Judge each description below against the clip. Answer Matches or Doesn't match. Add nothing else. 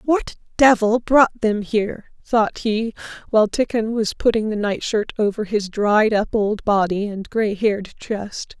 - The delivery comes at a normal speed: Matches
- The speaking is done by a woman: Matches